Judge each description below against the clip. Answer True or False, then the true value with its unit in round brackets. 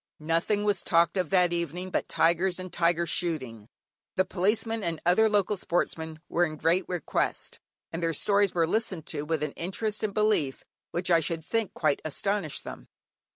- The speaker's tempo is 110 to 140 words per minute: False (175 wpm)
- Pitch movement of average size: True (3.3 semitones)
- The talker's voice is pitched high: False (175 Hz)